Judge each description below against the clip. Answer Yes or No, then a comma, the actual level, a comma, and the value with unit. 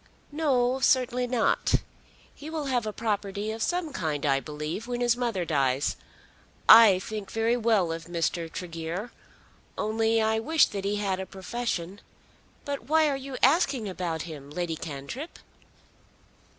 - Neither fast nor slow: Yes, average, 150 wpm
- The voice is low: No, high, 215 Hz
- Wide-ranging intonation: Yes, wide, 6.3 semitones